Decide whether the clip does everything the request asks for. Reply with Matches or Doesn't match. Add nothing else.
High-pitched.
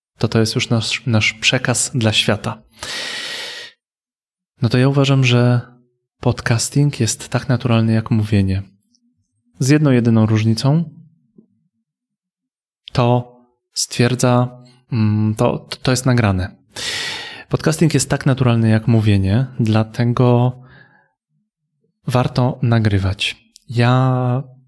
Doesn't match